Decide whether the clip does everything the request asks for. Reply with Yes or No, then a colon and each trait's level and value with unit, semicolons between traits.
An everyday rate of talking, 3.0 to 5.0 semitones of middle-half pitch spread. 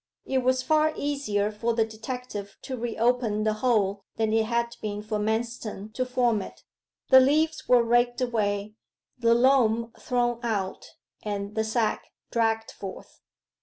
No: average, 155 wpm; narrow, 2.6 semitones